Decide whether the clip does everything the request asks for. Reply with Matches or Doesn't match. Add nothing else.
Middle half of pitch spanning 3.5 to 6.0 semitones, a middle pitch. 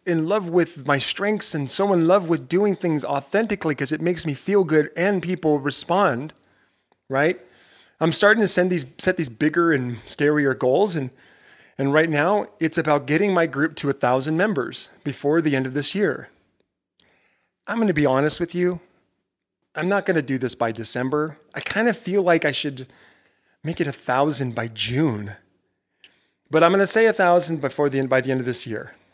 Matches